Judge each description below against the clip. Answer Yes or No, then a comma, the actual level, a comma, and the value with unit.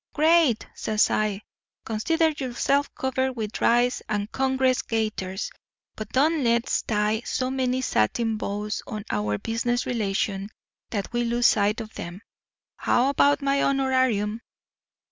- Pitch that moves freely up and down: No, average, 3.8 semitones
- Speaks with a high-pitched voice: Yes, high, 235 Hz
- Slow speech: Yes, slow, 130 wpm